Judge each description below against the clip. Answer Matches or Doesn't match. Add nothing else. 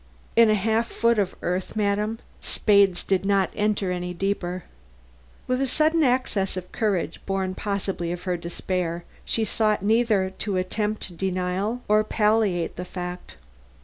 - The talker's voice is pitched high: Matches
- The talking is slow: Doesn't match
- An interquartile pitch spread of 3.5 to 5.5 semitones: Doesn't match